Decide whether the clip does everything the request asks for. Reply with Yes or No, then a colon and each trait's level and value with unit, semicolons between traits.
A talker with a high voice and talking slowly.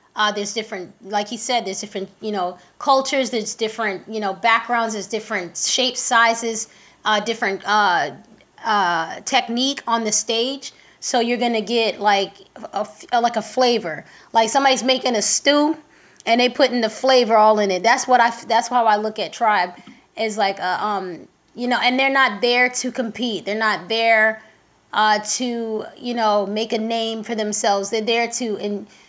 No: high, 225 Hz; average, 185 wpm